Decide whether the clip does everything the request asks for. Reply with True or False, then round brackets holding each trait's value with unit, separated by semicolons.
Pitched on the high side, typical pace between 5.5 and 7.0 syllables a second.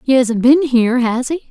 False (255 Hz; 5.0 syllables/s)